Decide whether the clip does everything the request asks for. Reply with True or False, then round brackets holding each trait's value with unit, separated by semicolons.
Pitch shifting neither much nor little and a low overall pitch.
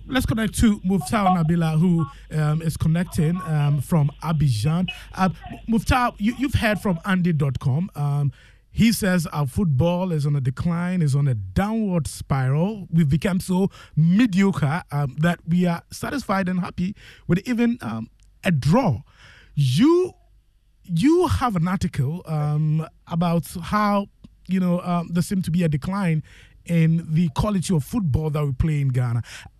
False (4.1 semitones; 170 Hz)